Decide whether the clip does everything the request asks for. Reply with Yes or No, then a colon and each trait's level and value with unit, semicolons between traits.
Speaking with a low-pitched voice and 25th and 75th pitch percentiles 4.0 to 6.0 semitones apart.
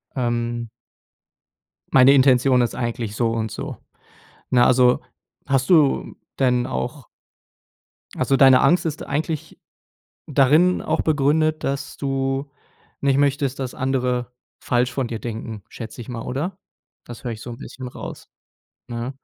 No: low, 130 Hz; narrow, 2.5 semitones